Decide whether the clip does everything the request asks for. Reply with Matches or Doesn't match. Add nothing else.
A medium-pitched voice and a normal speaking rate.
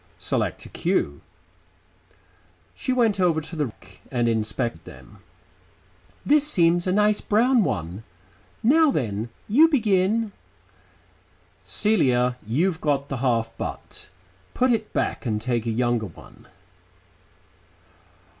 Doesn't match